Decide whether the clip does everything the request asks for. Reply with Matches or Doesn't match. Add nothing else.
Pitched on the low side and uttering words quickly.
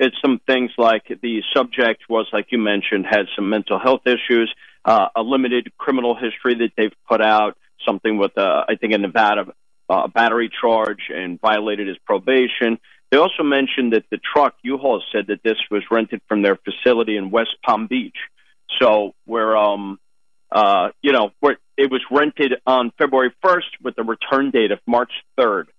Doesn't match